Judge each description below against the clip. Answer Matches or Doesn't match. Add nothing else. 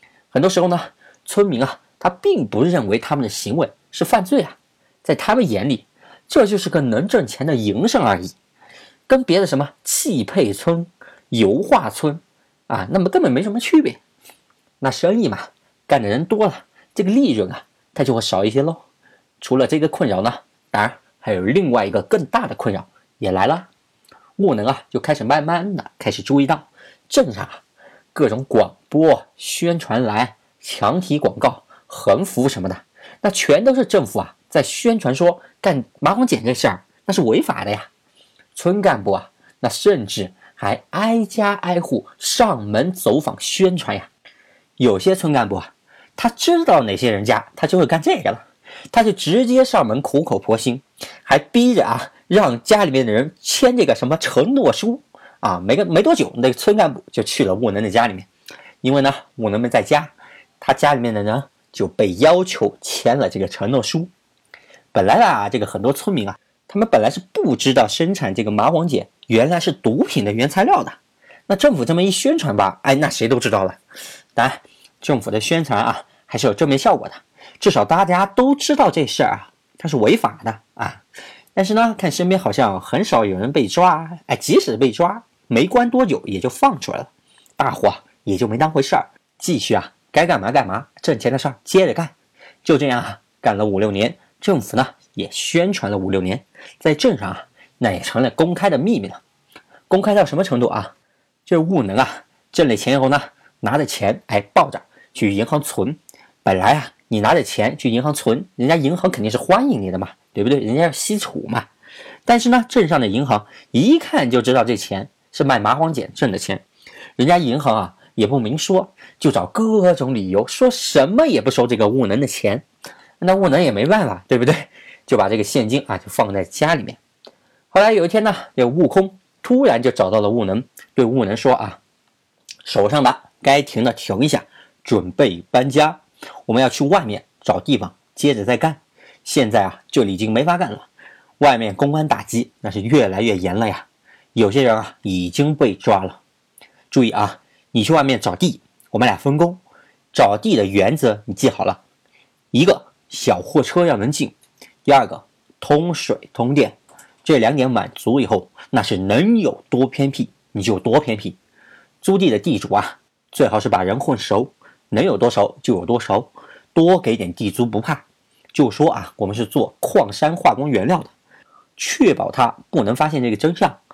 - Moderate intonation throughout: Doesn't match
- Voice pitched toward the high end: Doesn't match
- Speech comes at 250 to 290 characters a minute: Matches